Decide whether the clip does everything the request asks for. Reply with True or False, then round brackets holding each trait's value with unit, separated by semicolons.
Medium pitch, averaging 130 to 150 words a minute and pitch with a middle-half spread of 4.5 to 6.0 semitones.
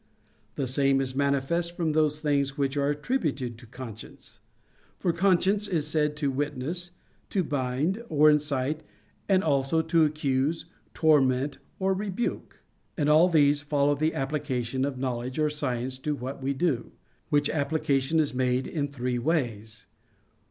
False (145 Hz; 145 wpm; 3.1 semitones)